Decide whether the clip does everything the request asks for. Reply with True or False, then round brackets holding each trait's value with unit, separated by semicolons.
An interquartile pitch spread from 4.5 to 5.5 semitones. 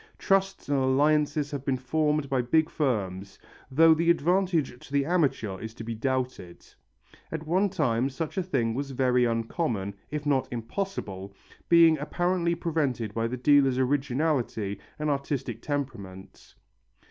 True (5.0 semitones)